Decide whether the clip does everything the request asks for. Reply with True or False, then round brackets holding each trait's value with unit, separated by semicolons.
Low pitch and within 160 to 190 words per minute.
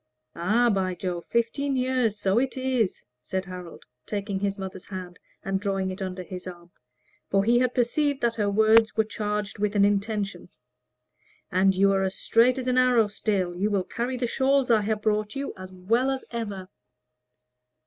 False (210 Hz; 180 wpm)